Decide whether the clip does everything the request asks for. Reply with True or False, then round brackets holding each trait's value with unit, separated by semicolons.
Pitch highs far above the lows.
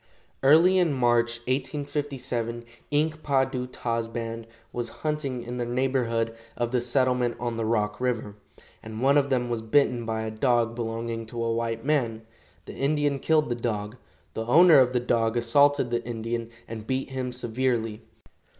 False (2.7 semitones)